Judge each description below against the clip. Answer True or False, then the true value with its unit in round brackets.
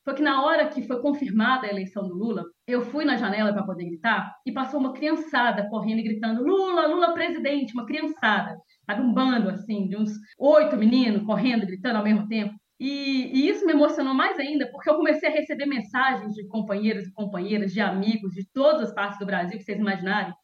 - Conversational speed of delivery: False (210 wpm)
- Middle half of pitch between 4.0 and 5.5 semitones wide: True (5.2 semitones)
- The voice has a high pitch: True (230 Hz)